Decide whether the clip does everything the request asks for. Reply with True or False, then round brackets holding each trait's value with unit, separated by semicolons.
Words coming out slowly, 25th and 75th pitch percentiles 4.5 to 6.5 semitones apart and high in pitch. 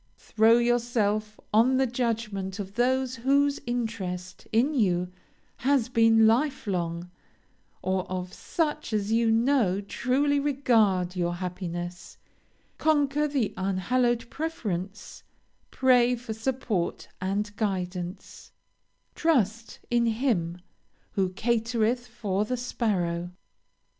True (105 wpm; 4.9 semitones; 225 Hz)